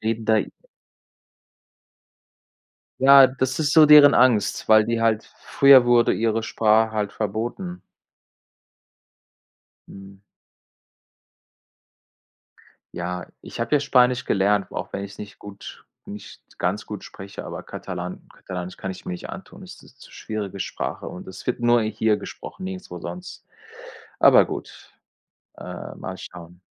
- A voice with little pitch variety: No, average, 4.1 semitones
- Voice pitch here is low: Yes, low, 110 Hz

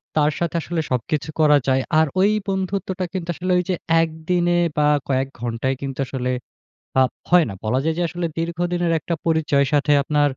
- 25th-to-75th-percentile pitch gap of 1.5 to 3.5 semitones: No, average, 4.1 semitones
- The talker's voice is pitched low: No, medium, 160 Hz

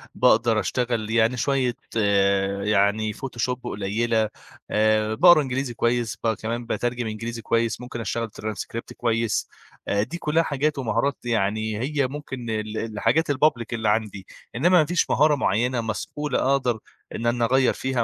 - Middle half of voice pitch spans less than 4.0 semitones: Yes, average, 3.1 semitones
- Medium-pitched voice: No, low, 115 Hz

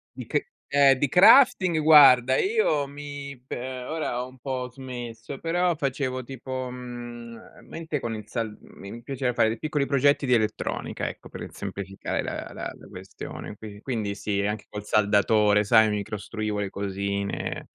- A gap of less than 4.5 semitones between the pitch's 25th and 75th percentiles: No, average, 4.8 semitones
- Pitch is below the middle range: Yes, low, 125 Hz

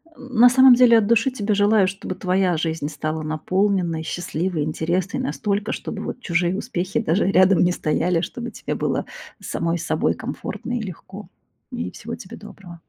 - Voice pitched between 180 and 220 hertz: Yes, medium, 185 Hz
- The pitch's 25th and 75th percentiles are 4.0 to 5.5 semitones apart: Yes, average, 4.3 semitones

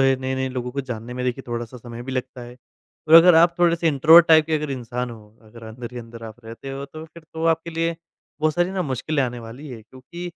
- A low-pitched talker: Yes, low, 130 Hz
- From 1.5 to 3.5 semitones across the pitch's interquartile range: No, average, 5.0 semitones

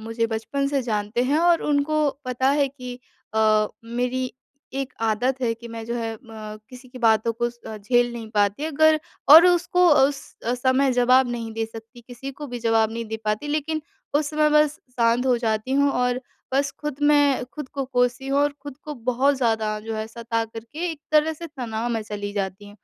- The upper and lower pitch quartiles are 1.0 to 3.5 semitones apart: No, average, 4.0 semitones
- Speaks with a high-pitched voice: Yes, very high, 250 Hz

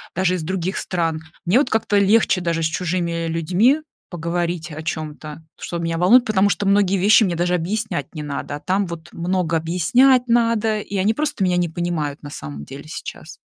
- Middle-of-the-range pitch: Yes, medium, 175 Hz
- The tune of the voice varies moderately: Yes, average, 3.6 semitones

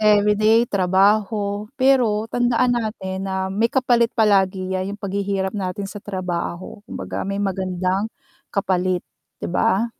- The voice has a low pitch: No, high, 200 Hz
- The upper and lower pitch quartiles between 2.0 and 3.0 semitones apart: Yes, narrow, 2.5 semitones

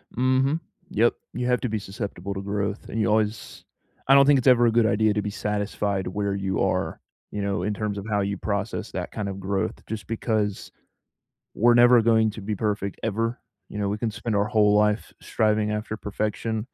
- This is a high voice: No, low, 105 Hz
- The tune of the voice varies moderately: No, narrow, 1.9 semitones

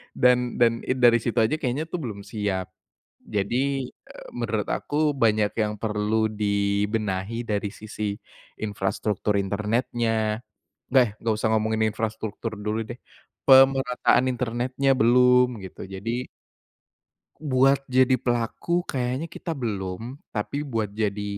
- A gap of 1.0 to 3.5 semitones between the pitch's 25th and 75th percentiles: Yes, average, 3.2 semitones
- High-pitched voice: No, low, 115 Hz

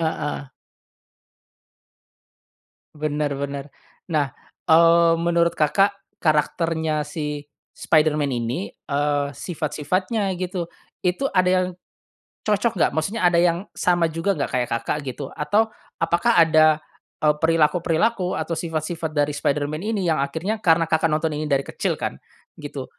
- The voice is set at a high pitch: No, medium, 160 Hz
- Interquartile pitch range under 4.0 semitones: Yes, average, 2.9 semitones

